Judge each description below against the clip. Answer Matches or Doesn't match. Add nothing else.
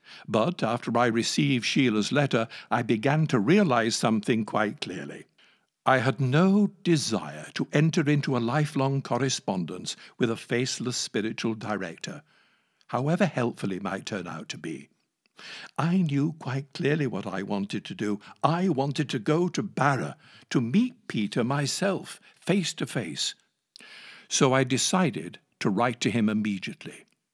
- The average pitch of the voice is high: Doesn't match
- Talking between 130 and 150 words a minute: Matches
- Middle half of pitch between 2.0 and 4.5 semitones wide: Doesn't match